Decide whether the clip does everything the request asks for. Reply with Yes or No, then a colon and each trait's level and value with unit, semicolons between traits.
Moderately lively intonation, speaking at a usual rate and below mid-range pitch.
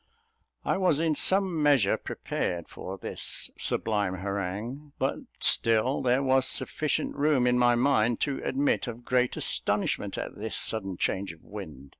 No: wide, 5.9 semitones; average, 150 wpm; low, 120 Hz